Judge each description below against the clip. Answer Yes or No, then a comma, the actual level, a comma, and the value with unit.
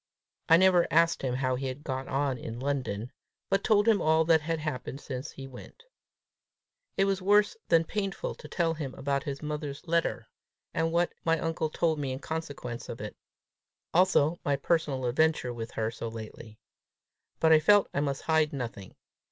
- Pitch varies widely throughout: No, average, 4.0 semitones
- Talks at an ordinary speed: Yes, average, 180 wpm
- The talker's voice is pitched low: No, medium, 150 Hz